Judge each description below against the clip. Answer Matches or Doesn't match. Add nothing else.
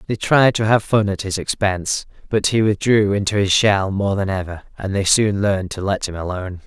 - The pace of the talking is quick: Matches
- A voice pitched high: Doesn't match